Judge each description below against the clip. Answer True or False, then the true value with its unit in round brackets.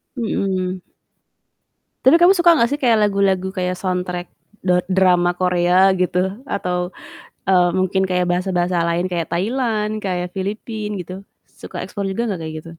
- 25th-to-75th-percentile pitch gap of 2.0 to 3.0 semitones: True (2.7 semitones)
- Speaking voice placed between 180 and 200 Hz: True (185 Hz)